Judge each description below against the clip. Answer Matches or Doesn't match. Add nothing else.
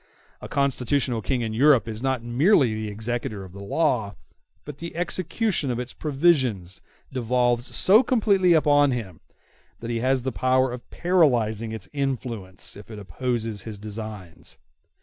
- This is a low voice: Matches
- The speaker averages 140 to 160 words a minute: Matches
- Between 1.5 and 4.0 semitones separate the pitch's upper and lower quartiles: Doesn't match